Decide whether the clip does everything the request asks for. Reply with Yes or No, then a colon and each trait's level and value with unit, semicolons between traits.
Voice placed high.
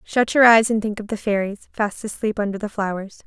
Yes: high, 210 Hz